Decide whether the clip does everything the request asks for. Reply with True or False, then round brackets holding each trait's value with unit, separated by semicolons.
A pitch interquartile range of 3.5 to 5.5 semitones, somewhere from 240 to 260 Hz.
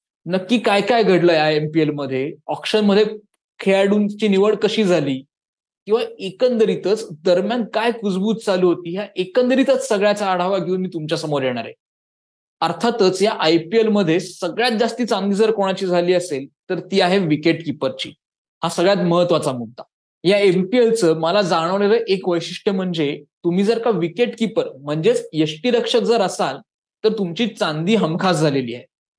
False (4.8 semitones; 190 Hz)